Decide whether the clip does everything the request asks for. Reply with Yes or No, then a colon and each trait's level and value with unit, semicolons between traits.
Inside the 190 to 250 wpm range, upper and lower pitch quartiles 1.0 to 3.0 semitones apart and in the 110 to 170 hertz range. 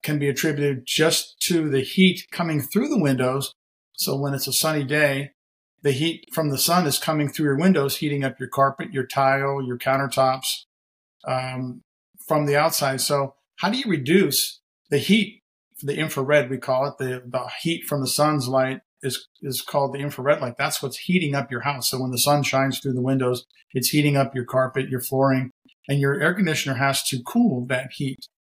Yes: average, 200 wpm; average, 2.7 semitones; medium, 140 Hz